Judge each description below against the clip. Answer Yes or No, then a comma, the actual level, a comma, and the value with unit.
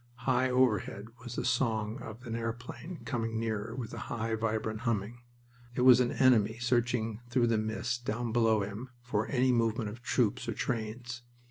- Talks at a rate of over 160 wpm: Yes, average, 170 wpm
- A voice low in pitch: Yes, low, 115 Hz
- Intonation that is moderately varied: No, narrow, 2.0 semitones